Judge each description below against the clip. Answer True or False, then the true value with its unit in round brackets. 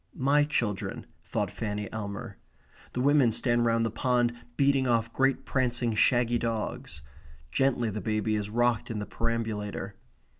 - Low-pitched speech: True (115 Hz)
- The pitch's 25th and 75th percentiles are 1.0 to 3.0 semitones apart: True (2.4 semitones)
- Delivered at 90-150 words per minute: True (145 wpm)